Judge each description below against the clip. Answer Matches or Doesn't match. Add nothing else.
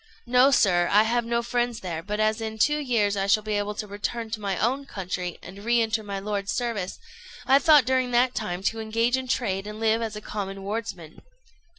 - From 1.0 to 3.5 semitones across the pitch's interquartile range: Matches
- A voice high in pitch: Matches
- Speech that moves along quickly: Matches